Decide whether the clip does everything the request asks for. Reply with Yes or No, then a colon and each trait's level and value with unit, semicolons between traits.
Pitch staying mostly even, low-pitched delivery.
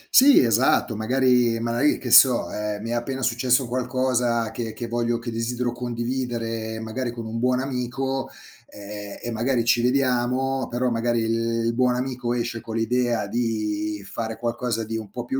Yes: narrow, 1.7 semitones; low, 120 Hz